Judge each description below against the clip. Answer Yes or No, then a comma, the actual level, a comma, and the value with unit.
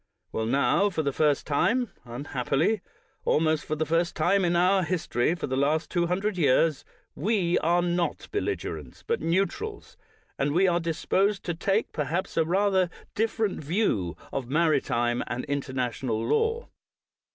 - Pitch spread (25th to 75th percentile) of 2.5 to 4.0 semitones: No, average, 5.3 semitones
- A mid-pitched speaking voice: Yes, medium, 165 Hz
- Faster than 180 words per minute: No, average, 160 wpm